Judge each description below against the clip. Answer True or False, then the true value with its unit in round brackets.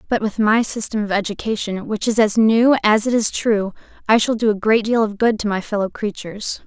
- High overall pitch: True (215 Hz)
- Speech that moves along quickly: True (235 wpm)